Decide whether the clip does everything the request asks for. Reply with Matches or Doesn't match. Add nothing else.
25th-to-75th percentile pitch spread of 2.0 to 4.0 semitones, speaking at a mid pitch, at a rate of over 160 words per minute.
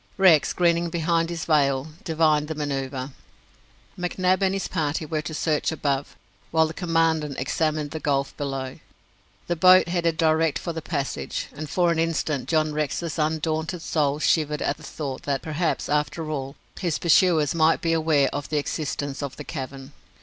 Matches